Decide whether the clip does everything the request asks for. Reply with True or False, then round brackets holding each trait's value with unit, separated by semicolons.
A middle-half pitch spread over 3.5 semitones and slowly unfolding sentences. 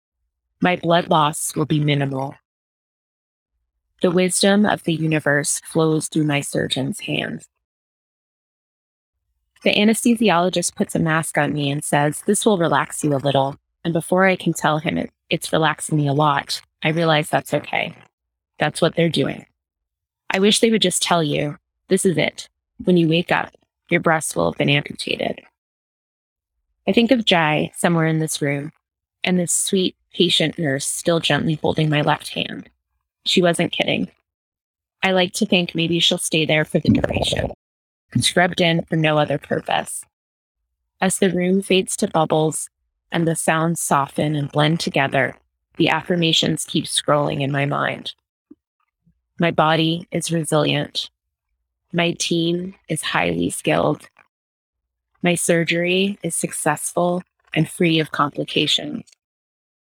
False (4.2 semitones; 145 wpm)